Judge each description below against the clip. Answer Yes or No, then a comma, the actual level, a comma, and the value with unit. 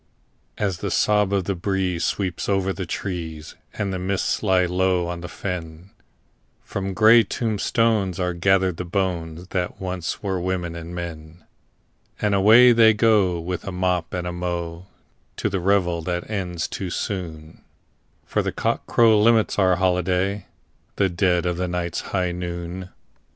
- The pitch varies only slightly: Yes, narrow, 2.1 semitones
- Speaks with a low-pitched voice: Yes, very low, 90 Hz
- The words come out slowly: No, average, 150 wpm